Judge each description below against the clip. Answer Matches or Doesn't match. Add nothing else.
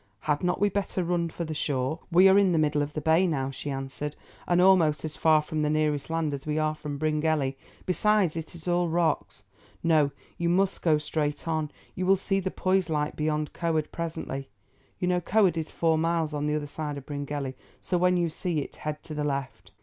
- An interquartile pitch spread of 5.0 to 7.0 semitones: Doesn't match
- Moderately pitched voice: Matches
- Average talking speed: Doesn't match